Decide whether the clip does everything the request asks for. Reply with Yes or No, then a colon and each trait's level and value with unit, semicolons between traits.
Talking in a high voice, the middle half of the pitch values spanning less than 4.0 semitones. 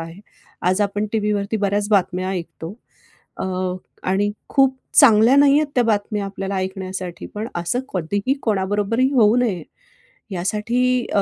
Yes: high, 205 Hz; average, 3.3 semitones